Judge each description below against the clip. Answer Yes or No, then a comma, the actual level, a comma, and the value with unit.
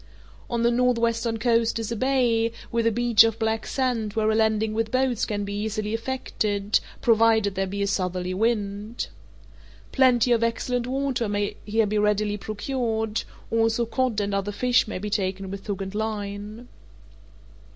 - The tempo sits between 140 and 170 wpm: Yes, average, 165 wpm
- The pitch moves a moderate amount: No, narrow, 2.3 semitones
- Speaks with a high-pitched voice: Yes, high, 220 Hz